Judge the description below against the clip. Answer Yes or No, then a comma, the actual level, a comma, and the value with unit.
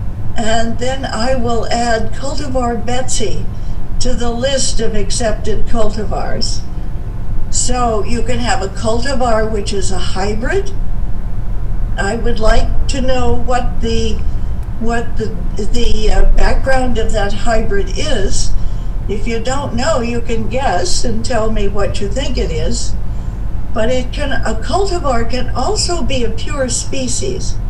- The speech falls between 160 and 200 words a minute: No, average, 140 wpm